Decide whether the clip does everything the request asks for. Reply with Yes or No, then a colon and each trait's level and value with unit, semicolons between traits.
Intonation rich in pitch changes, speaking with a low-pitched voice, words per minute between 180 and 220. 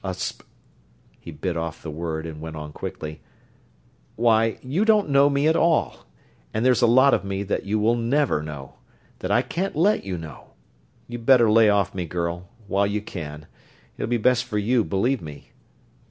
Yes: wide, 7.3 semitones; low, 105 Hz; average, 190 wpm